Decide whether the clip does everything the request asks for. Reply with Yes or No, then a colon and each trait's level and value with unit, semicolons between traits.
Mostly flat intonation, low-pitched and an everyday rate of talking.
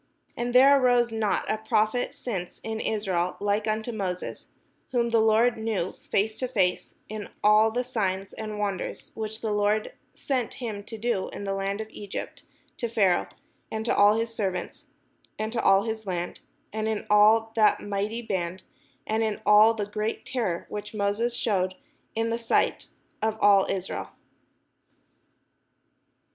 No: narrow, 1.9 semitones; high, 215 Hz; average, 160 wpm